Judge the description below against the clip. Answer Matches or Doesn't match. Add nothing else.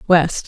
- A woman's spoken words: Matches